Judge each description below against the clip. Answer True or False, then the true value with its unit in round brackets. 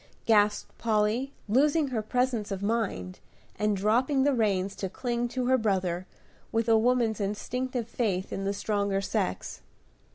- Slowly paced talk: False (150 wpm)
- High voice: True (220 Hz)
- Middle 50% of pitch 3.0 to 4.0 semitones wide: True (3.7 semitones)